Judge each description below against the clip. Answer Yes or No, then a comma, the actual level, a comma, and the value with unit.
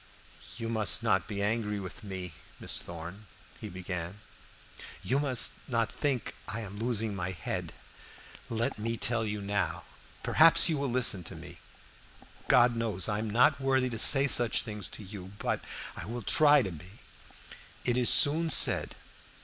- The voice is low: Yes, low, 110 Hz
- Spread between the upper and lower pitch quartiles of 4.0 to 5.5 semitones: No, average, 3.6 semitones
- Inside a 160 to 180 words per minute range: Yes, average, 165 wpm